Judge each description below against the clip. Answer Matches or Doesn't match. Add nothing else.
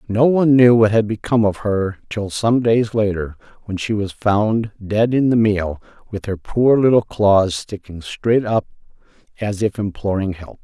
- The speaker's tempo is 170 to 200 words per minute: Matches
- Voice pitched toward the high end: Doesn't match